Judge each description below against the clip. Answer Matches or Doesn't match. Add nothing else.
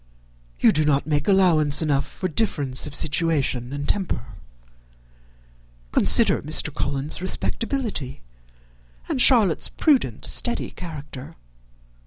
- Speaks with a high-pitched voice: Doesn't match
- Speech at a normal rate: Doesn't match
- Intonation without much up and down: Doesn't match